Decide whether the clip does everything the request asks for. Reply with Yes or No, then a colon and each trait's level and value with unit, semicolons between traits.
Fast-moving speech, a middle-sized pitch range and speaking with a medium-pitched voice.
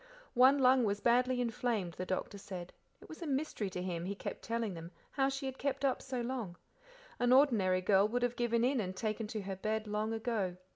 No: fast, 220 wpm; average, 4.6 semitones; high, 225 Hz